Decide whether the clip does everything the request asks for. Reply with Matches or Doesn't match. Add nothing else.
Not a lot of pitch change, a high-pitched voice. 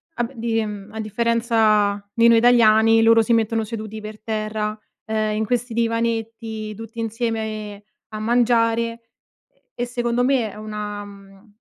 Matches